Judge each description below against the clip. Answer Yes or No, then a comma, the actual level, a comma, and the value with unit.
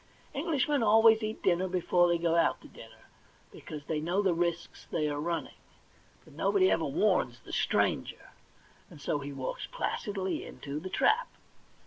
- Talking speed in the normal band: Yes, average, 160 wpm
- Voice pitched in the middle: Yes, medium, 175 Hz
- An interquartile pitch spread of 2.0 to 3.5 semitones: No, average, 5.2 semitones